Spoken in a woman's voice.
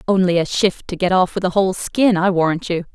Yes: female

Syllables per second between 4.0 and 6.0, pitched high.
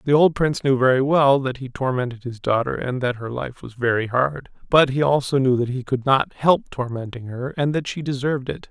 No: 5.4 syllables/s; low, 130 Hz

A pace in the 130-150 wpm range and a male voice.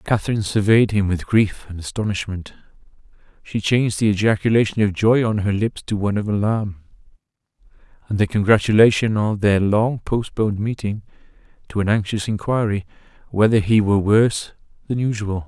Yes: average, 145 wpm; male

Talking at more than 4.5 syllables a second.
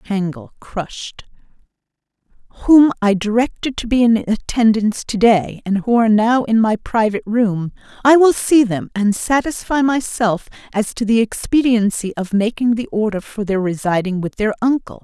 Yes: 4.9 syllables/s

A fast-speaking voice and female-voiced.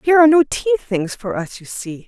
Yes: fast, 260 wpm; female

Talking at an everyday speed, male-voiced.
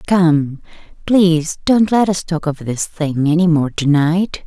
No: average, 175 wpm; female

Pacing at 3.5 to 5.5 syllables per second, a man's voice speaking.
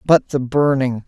Yes: 4.4 syllables/s; male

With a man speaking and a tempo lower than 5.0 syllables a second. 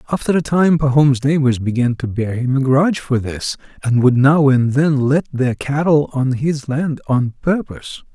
Yes: male; 4.6 syllables/s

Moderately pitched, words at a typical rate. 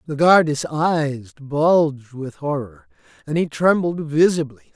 No: medium, 150 Hz; slow, 125 wpm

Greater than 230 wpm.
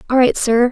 Yes: fast, 250 wpm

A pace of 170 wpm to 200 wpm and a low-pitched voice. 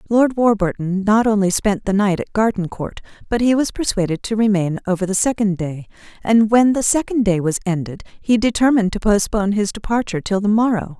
No: average, 190 wpm; high, 205 Hz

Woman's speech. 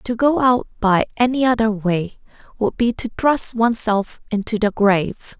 Yes: female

